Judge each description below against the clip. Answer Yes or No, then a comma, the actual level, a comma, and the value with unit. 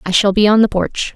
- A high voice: Yes, high, 200 Hz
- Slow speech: No, fast, 310 wpm